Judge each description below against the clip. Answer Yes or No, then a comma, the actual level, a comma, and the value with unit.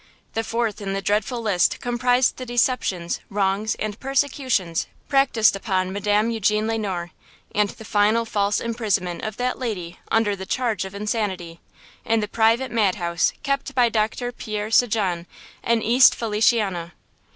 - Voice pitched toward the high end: Yes, high, 215 Hz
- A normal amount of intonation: Yes, average, 3.1 semitones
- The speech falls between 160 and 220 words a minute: No, average, 150 wpm